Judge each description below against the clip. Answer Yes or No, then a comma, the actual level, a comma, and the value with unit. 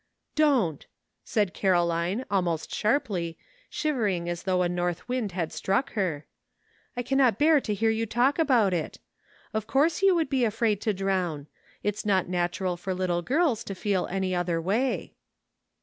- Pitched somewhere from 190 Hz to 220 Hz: Yes, high, 200 Hz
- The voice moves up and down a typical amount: No, wide, 5.7 semitones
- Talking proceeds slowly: No, average, 170 wpm